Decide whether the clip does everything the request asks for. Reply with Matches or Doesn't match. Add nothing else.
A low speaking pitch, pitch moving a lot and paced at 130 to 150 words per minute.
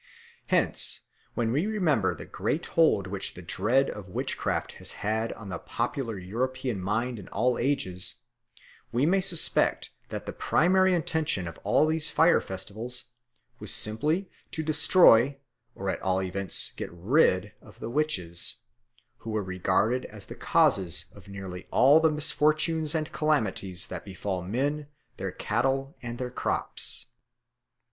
Matches